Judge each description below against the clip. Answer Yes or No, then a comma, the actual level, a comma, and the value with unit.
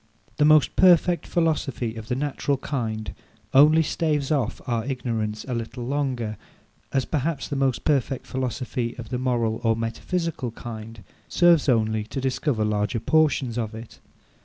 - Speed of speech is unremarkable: Yes, average, 150 wpm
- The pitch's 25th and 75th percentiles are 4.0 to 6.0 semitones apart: Yes, average, 4.3 semitones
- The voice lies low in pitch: Yes, low, 125 Hz